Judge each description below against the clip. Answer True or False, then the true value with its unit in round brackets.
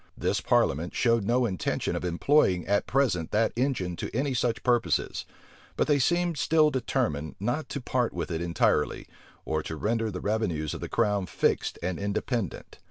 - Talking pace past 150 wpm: True (170 wpm)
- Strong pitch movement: True (6.4 semitones)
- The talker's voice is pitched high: False (110 Hz)